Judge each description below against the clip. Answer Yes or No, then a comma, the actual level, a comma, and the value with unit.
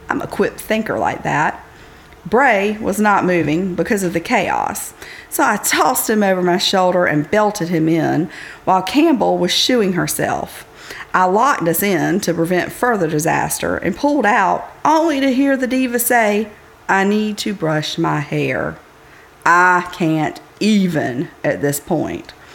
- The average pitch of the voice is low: No, medium, 185 Hz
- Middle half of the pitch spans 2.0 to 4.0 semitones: No, average, 4.8 semitones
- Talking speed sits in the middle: Yes, average, 155 wpm